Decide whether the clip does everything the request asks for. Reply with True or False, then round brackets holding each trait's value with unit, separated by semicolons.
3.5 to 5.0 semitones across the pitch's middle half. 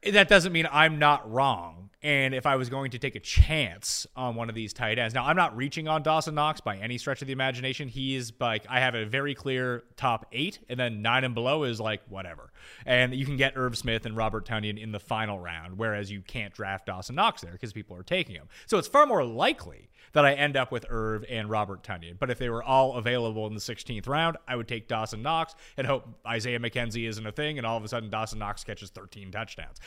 True (3.9 semitones)